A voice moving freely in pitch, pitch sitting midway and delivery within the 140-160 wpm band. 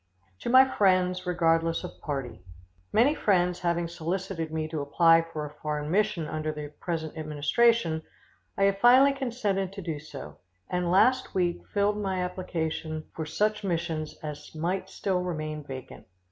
No: average, 3.9 semitones; medium, 170 Hz; average, 155 wpm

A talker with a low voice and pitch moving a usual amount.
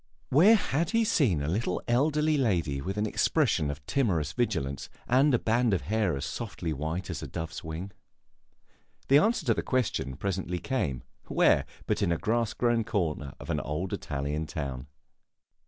No: very low, 95 Hz; wide, 8.1 semitones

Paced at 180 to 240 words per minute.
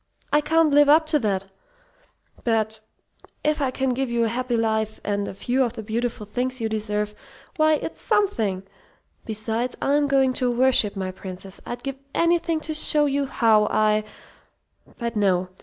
No: average, 170 wpm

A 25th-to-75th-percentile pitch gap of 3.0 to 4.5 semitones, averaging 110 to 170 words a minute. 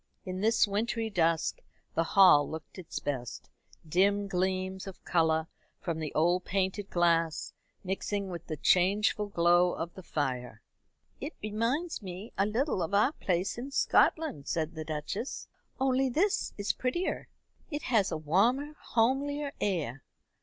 No: wide, 5.4 semitones; average, 145 wpm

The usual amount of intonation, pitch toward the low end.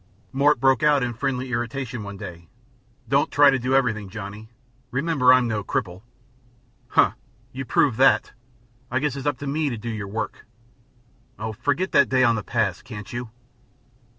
Yes: average, 3.9 semitones; low, 125 Hz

